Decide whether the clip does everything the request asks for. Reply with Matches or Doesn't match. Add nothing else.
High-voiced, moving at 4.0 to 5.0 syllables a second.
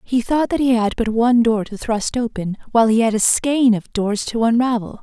Doesn't match